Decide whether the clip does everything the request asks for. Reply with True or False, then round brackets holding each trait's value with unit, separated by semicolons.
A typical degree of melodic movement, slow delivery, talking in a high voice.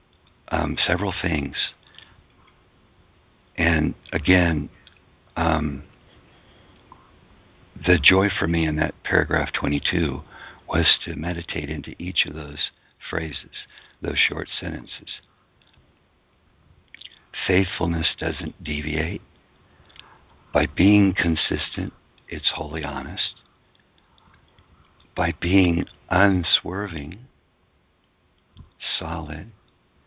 False (3.4 semitones; 75 wpm; 85 Hz)